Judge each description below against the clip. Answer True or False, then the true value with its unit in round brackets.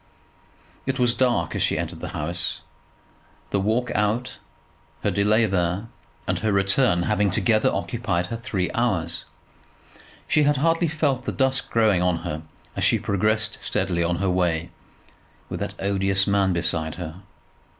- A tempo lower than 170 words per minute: True (150 wpm)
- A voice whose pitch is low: True (100 Hz)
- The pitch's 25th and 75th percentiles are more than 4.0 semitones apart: True (4.9 semitones)